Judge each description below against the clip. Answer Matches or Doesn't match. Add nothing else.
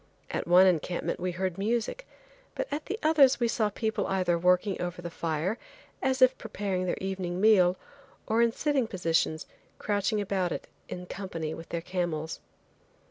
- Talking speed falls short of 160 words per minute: Doesn't match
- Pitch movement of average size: Matches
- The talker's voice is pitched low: Doesn't match